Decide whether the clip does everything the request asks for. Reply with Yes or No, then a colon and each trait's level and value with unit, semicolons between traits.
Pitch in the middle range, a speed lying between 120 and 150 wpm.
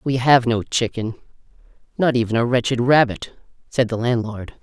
No: low, 120 Hz; average, 145 wpm